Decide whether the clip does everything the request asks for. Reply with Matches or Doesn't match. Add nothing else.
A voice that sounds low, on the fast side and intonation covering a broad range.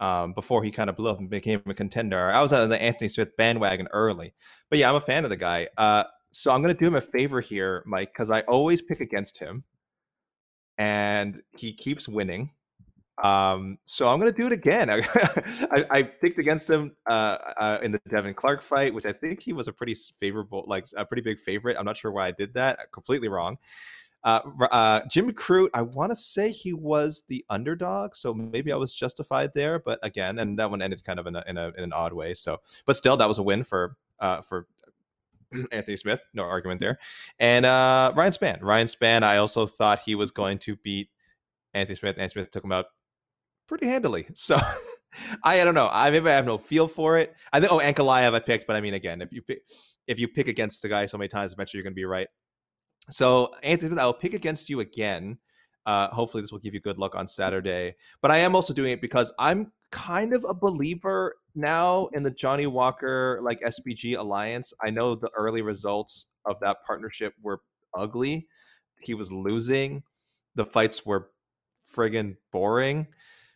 Matches